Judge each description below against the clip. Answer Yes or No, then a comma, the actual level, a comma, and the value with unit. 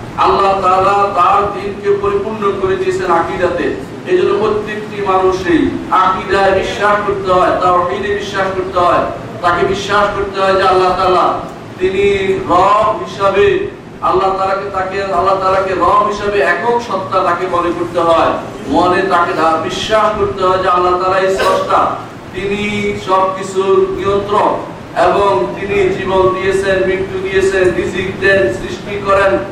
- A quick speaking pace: Yes, fast, 130 wpm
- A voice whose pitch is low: No, high, 190 Hz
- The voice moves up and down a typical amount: No, narrow, 1.3 semitones